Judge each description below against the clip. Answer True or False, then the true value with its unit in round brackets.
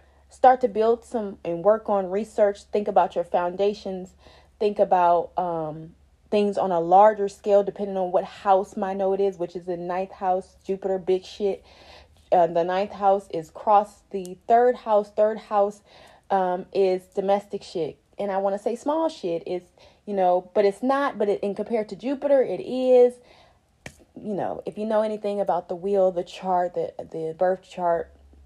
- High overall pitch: True (195 Hz)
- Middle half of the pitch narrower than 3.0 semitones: True (2.5 semitones)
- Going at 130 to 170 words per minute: False (180 wpm)